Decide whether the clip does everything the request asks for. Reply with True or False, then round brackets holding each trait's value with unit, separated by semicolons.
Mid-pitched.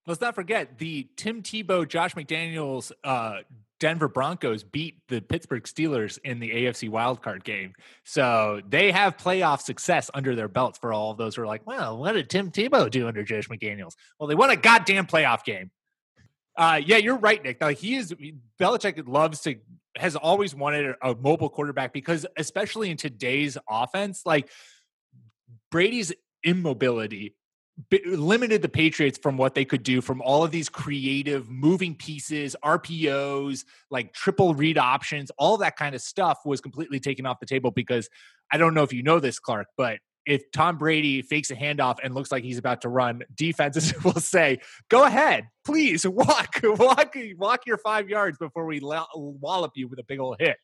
True (150 Hz)